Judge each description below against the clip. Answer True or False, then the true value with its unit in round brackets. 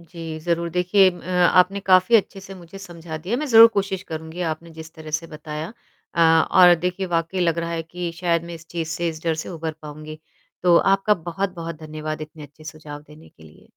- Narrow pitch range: True (2.3 semitones)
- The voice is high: False (170 Hz)